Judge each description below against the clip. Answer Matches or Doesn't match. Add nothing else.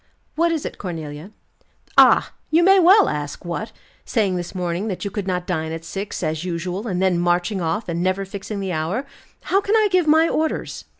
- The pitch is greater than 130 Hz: Matches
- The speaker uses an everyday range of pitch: Doesn't match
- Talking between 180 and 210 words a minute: Matches